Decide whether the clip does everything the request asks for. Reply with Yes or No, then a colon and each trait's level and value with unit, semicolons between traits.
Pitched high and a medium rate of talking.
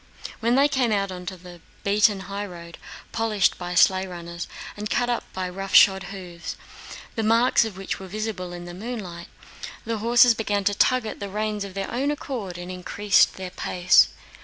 Yes: high, 200 Hz; average, 175 wpm